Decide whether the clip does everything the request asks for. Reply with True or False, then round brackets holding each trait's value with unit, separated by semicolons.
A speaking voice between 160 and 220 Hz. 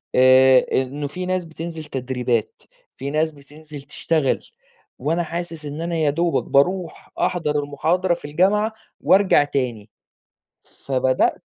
False (150 Hz)